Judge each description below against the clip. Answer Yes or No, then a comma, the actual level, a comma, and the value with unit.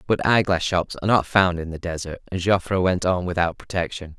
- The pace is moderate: No, fast, 215 wpm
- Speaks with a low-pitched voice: Yes, very low, 90 Hz